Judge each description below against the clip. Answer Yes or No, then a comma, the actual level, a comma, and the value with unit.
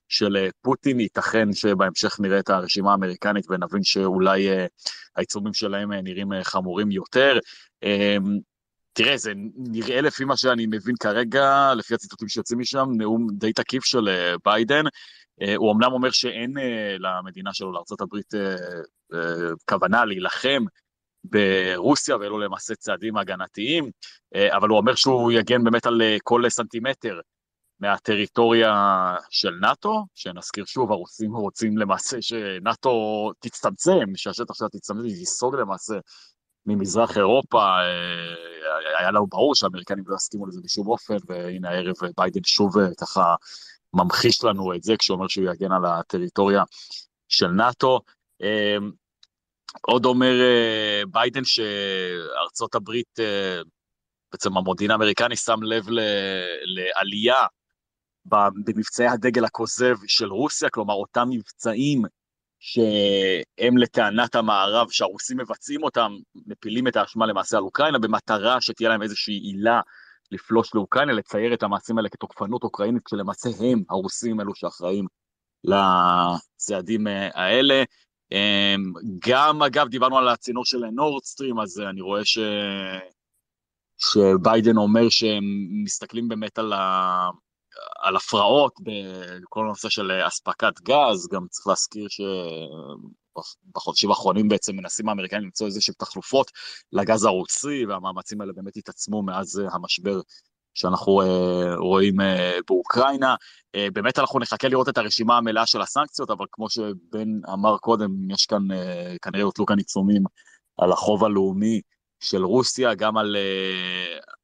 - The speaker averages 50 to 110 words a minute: No, average, 125 wpm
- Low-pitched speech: Yes, low, 105 Hz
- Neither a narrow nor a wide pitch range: Yes, average, 3.2 semitones